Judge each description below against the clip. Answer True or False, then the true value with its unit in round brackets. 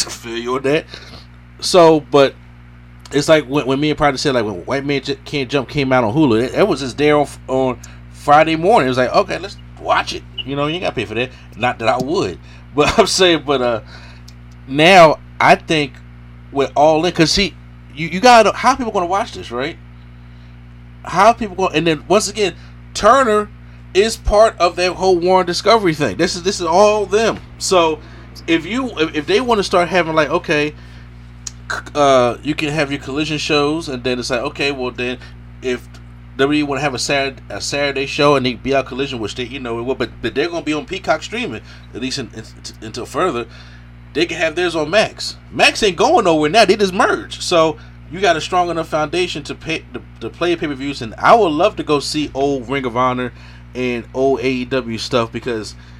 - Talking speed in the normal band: False (215 wpm)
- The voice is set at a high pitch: False (135 Hz)